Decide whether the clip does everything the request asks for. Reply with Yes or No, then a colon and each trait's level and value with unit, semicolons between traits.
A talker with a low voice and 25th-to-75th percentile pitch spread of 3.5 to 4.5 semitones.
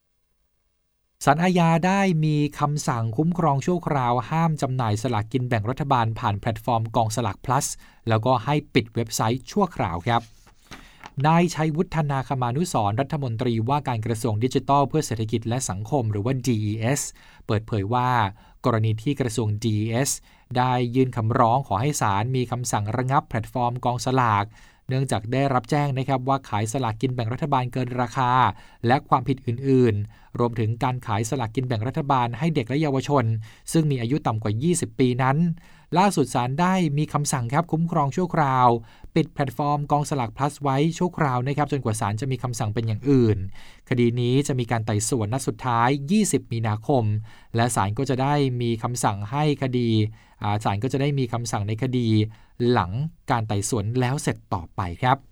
Yes: low, 125 Hz; average, 4.0 semitones